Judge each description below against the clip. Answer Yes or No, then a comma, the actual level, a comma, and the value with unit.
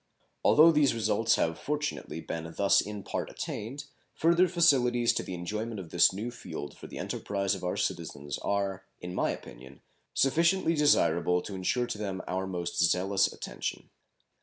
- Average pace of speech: Yes, average, 160 wpm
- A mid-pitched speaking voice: No, low, 100 Hz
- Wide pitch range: Yes, wide, 6.3 semitones